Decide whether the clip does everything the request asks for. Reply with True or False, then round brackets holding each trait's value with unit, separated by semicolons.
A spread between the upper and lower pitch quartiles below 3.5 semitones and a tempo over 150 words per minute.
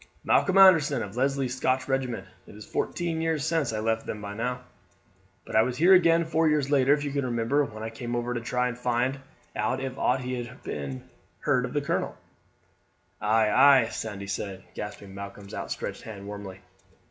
False (4.5 semitones; 180 wpm)